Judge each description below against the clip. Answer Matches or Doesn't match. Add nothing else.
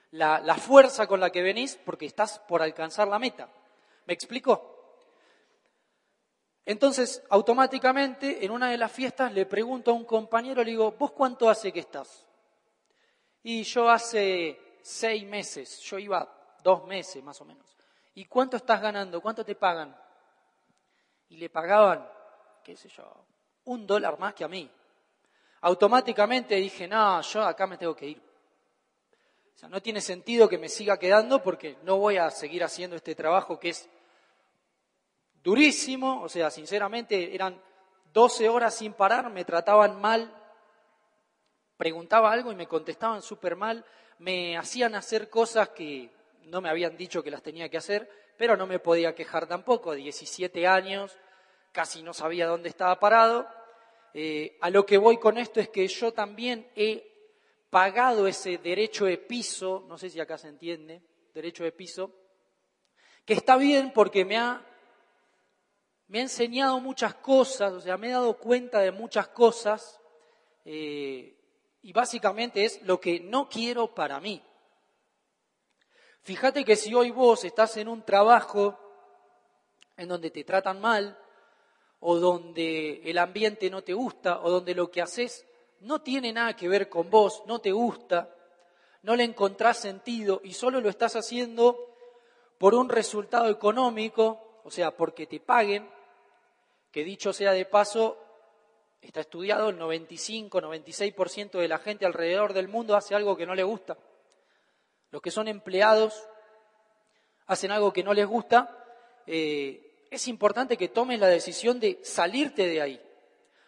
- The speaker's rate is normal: Matches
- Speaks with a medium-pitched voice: Doesn't match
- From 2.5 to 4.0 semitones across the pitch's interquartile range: Doesn't match